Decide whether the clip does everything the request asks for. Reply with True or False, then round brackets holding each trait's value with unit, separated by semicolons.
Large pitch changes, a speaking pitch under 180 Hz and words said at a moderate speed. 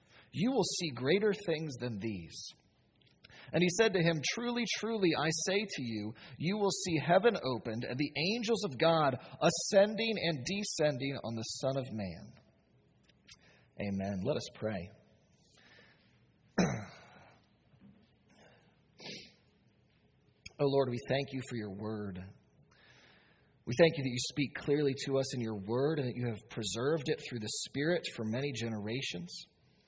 True (6.6 semitones; 140 Hz; 145 wpm)